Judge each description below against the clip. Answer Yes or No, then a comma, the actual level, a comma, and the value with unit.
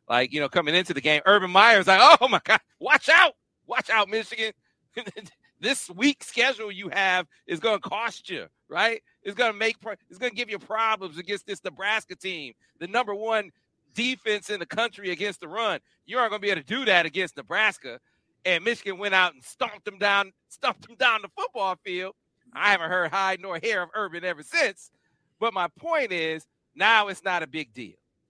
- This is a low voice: No, high, 200 Hz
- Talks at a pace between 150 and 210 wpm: Yes, average, 200 wpm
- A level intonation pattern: No, average, 3.7 semitones